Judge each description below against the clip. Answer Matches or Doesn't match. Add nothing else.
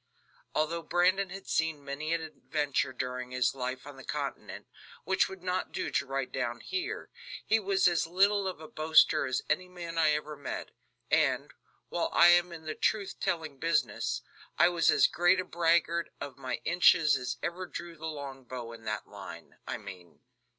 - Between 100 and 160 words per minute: Doesn't match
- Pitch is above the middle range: Doesn't match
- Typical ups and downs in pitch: Matches